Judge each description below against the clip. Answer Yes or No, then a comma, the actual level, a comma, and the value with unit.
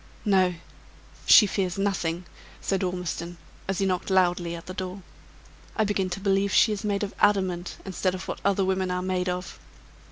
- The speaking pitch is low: No, medium, 185 Hz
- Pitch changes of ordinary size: No, narrow, 1.4 semitones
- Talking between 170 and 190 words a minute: Yes, average, 180 wpm